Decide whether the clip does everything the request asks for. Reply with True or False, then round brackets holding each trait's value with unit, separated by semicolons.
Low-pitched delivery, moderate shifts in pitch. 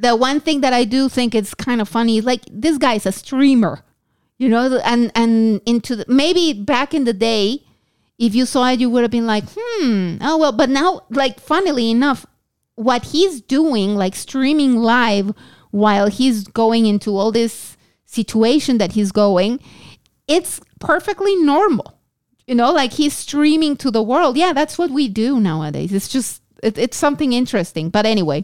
False (245 Hz; 4.7 semitones)